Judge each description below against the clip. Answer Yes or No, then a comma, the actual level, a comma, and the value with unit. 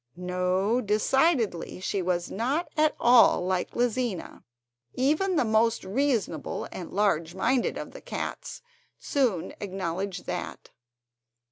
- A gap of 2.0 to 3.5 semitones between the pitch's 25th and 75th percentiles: No, wide, 5.6 semitones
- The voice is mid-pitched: No, high, 210 Hz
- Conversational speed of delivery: No, slow, 115 wpm